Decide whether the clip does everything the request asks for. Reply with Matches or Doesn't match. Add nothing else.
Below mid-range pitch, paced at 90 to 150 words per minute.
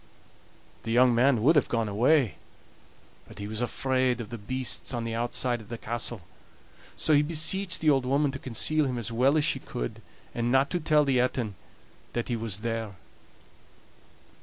Doesn't match